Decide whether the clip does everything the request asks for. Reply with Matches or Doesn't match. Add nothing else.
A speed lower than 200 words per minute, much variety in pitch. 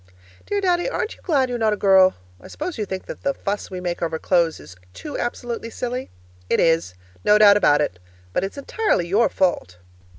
Doesn't match